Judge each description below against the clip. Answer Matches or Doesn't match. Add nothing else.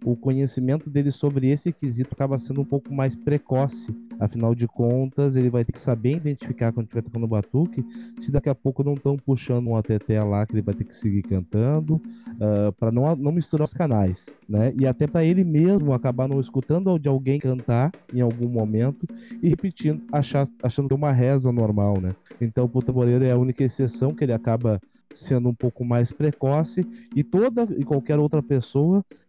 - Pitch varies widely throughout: Doesn't match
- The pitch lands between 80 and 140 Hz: Matches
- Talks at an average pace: Doesn't match